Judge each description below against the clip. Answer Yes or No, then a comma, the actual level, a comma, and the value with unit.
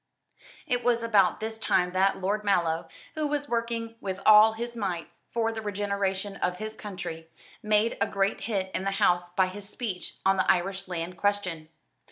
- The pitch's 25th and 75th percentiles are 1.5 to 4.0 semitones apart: Yes, average, 3.1 semitones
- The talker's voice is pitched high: Yes, high, 200 Hz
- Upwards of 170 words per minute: Yes, average, 180 wpm